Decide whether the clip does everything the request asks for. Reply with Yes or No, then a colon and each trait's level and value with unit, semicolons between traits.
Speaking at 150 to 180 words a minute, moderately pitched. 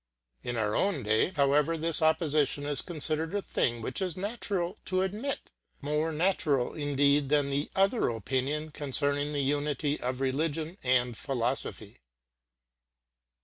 No: average, 140 wpm; medium, 145 Hz